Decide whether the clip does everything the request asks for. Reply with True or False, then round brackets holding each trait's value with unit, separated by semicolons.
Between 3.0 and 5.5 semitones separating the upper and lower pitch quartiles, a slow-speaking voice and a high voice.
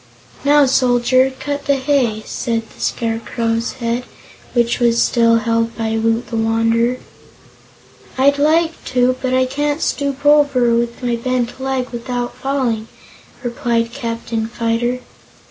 False (2.4 semitones; 130 wpm; 240 Hz)